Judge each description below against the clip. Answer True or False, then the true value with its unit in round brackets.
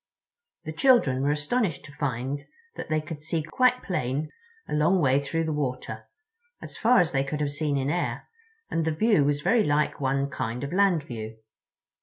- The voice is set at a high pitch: False (150 Hz)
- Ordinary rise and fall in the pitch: True (4.3 semitones)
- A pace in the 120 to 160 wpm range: False (185 wpm)